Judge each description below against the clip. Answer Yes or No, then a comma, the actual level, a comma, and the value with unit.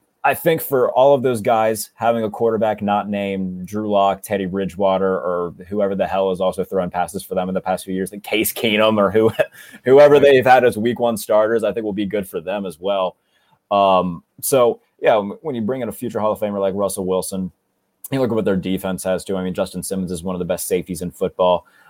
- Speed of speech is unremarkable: No, fast, 240 wpm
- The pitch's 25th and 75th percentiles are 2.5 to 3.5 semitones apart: Yes, average, 2.9 semitones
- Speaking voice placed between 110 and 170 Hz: No, low, 100 Hz